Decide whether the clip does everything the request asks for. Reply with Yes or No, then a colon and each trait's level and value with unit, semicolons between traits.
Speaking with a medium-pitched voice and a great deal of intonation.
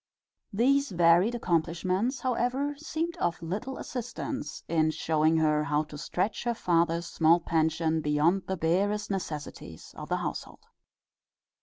Yes: medium, 175 Hz; wide, 6.7 semitones